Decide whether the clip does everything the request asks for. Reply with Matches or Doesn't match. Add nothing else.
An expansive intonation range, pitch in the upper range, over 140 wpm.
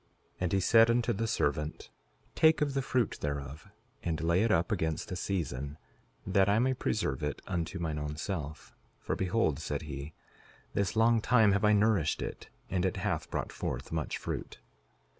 Doesn't match